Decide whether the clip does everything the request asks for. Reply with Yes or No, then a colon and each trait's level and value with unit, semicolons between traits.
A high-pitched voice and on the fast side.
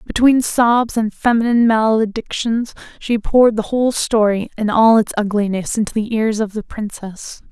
No: high, 220 Hz; average, 160 wpm